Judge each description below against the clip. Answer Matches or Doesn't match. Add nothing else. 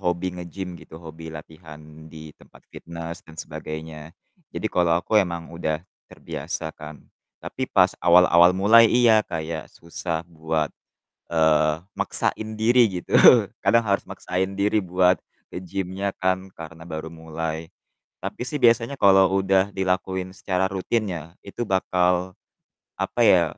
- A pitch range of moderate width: Matches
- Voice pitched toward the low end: Matches